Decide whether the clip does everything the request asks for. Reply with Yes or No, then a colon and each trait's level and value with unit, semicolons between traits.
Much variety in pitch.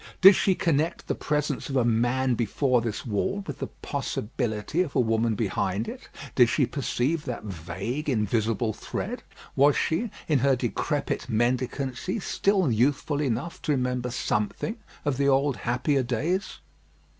No: average, 4.2 semitones